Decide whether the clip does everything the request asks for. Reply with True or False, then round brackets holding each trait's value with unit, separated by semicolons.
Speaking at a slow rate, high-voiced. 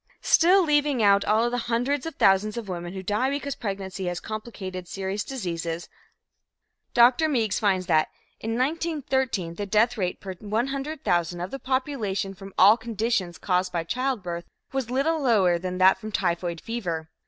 False (160 wpm; 210 Hz)